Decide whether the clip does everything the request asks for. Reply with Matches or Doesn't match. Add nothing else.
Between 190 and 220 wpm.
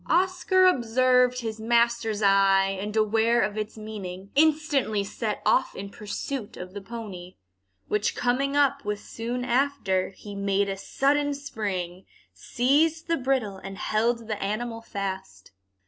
Doesn't match